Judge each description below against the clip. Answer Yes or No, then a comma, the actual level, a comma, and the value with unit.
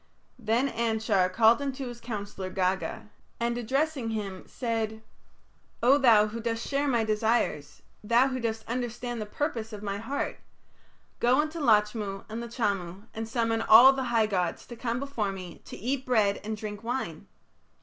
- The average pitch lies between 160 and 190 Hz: No, high, 225 Hz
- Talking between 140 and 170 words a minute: Yes, average, 160 wpm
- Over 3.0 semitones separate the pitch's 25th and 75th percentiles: No, average, 2.7 semitones